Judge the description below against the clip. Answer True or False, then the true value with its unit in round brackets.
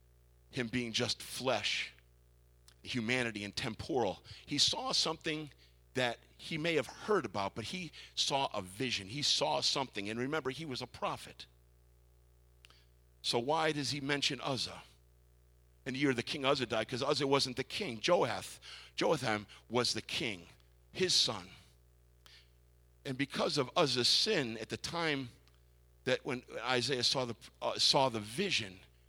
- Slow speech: False (150 wpm)